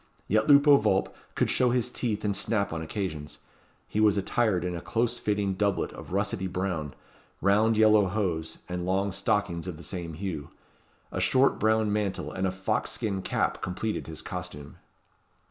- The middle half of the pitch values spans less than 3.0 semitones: No, average, 3.3 semitones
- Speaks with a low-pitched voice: Yes, low, 100 Hz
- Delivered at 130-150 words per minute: No, average, 170 wpm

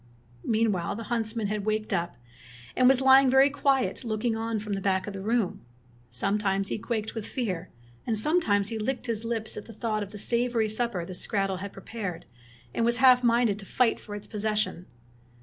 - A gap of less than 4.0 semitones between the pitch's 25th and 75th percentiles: Yes, average, 2.8 semitones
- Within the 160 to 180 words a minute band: No, average, 190 wpm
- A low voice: No, high, 220 Hz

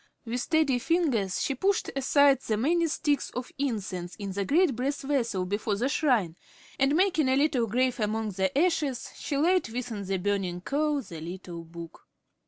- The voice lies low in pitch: No, high, 245 Hz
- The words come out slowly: No, average, 175 wpm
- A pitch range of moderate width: No, wide, 6.4 semitones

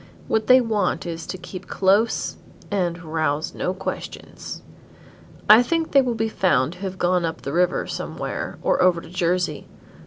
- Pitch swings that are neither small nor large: Yes, average, 4.0 semitones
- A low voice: No, medium, 185 Hz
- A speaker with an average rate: Yes, average, 165 wpm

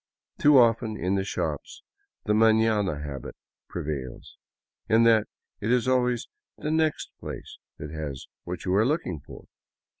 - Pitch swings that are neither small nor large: No, wide, 7.1 semitones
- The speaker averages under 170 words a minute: Yes, average, 150 wpm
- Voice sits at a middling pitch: No, low, 105 Hz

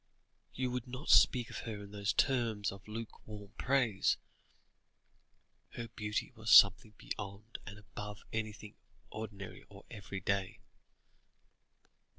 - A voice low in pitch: Yes, low, 105 Hz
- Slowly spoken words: Yes, slow, 115 wpm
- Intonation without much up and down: Yes, narrow, 2.3 semitones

